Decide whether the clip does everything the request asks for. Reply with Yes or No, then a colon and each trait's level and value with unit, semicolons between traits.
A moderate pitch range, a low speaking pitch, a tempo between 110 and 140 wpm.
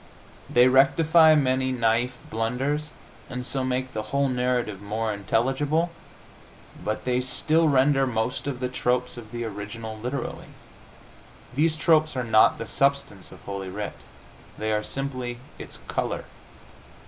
Yes: average, 3.7 semitones; low, 125 Hz; slow, 135 wpm